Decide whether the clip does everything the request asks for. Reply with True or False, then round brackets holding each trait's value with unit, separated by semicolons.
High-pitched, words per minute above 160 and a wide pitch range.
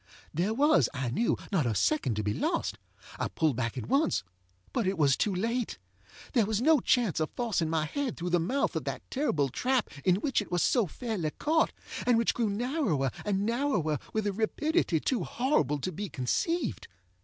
True (200 Hz; 190 wpm; 8.4 semitones)